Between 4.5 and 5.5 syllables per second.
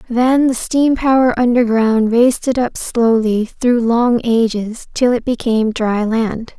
No: 4.0 syllables/s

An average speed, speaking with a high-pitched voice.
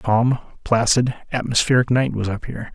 No: average, 155 wpm; low, 120 Hz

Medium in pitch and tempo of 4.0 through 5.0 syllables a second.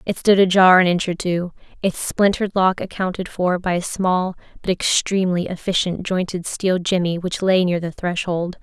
Yes: medium, 180 Hz; 4.9 syllables/s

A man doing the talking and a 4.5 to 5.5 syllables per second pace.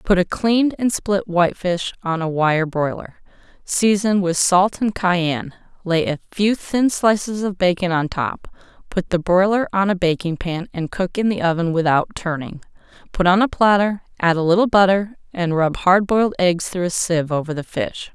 No: female; 4.9 syllables/s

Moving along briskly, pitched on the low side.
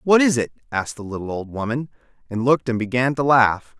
Yes: fast, 220 wpm; low, 125 Hz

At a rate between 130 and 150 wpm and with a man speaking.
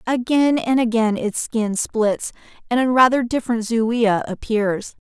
No: average, 140 wpm; female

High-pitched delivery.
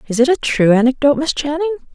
Yes: very high, 270 Hz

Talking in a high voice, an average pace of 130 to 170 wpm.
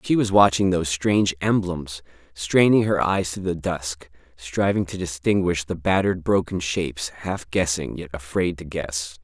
No: very low, 85 Hz; average, 160 wpm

